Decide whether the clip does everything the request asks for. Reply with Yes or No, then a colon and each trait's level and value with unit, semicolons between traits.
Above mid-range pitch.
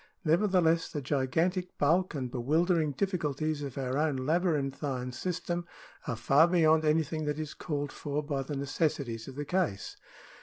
No: medium, 150 Hz